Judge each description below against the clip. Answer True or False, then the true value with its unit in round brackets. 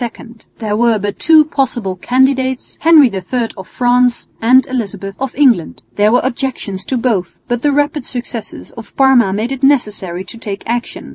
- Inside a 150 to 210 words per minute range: True (165 wpm)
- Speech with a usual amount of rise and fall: True (4.0 semitones)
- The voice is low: False (240 Hz)